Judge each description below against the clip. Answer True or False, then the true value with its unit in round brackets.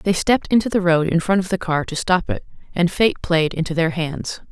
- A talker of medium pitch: True (175 Hz)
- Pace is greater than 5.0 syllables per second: True (5.5 syllables/s)